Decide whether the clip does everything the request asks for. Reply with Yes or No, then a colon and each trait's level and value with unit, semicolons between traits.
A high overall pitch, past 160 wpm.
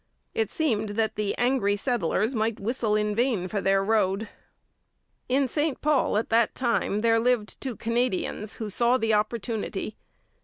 No: high, 225 Hz; average, 155 wpm